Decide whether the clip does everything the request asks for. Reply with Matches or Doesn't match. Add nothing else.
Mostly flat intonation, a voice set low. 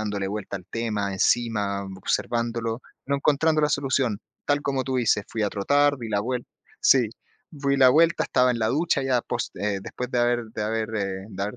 Doesn't match